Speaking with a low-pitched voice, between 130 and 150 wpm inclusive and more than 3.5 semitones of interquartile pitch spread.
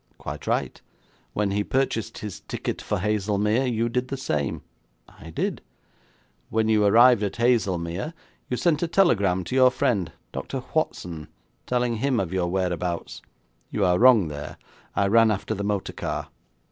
No: low, 105 Hz; average, 160 wpm; average, 5.1 semitones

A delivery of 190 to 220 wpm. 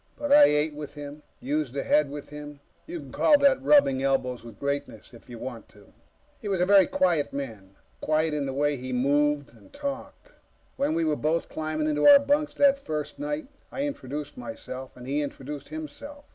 Yes: average, 200 wpm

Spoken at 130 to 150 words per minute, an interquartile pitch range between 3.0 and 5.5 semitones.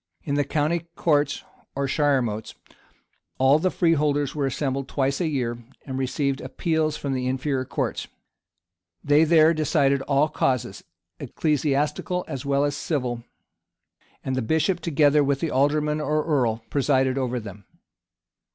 No: average, 140 wpm; narrow, 2.4 semitones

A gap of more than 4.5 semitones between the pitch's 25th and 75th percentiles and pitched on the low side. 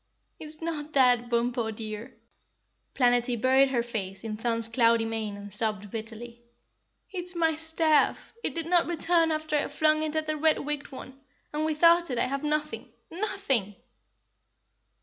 No: wide, 5.4 semitones; very high, 270 Hz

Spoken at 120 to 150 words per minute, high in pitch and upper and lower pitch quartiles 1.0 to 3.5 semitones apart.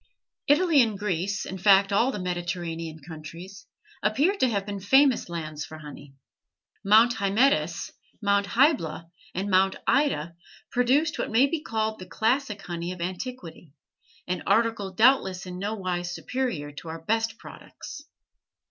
No: average, 140 wpm; high, 200 Hz; average, 5.2 semitones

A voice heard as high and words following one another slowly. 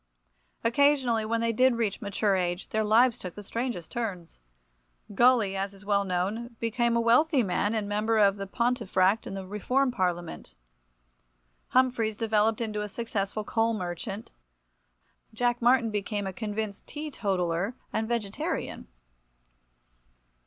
Yes: high, 215 Hz; slow, 130 wpm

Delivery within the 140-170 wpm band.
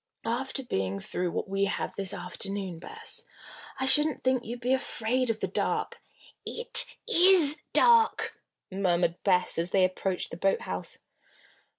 Yes: average, 145 wpm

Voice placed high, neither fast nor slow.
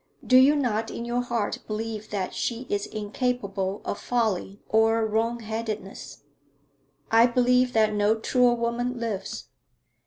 No: high, 225 Hz; slow, 130 wpm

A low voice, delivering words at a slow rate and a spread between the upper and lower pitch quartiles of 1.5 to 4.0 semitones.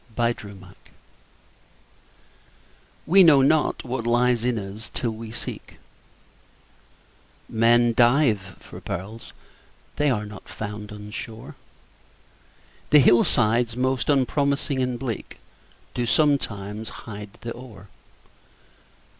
Yes: low, 115 Hz; slow, 100 wpm; average, 3.5 semitones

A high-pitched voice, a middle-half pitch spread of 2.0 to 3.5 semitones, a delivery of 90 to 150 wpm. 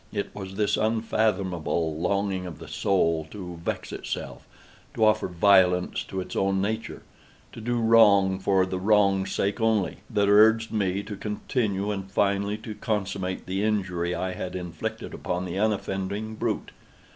No: low, 100 Hz; narrow, 2.4 semitones; average, 145 wpm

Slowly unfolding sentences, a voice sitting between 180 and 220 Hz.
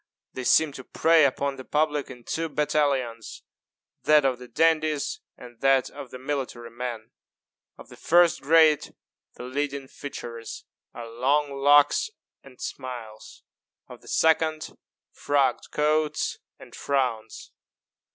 No: slow, 130 wpm; medium, 140 Hz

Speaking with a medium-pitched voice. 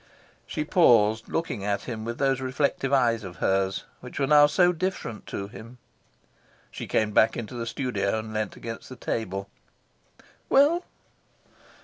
No: low, 115 Hz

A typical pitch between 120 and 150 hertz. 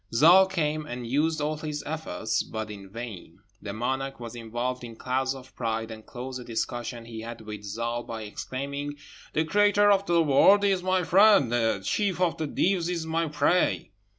Yes: low, 135 Hz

